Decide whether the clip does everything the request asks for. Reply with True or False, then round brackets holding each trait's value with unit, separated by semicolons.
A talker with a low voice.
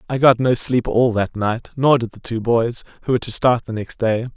True (120 Hz)